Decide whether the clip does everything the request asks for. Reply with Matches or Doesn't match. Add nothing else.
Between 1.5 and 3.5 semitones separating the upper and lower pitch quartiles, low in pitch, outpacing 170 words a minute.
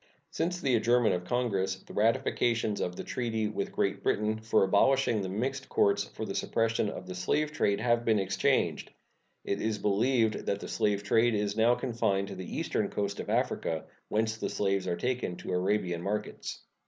Matches